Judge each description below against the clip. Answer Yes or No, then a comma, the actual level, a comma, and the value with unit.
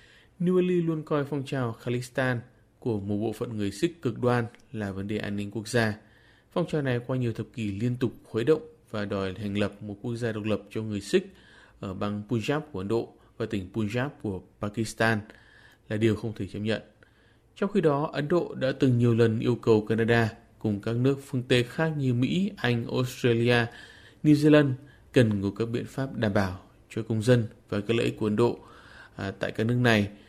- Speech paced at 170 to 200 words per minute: No, average, 210 wpm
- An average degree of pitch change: Yes, average, 3.3 semitones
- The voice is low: Yes, low, 115 Hz